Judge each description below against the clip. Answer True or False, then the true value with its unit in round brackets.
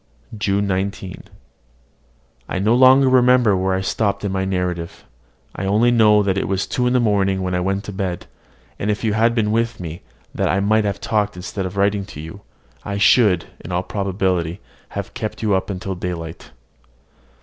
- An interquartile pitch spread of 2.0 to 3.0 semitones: True (2.5 semitones)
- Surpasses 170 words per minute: True (185 wpm)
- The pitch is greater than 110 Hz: False (100 Hz)